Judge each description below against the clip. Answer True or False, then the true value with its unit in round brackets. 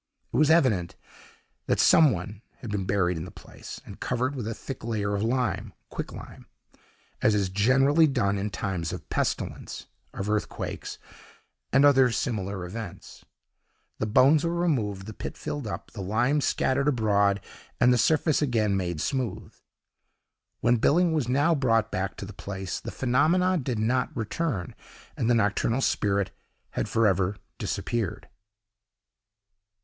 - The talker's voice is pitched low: True (115 Hz)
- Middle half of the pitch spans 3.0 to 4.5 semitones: False (5.1 semitones)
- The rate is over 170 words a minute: False (150 wpm)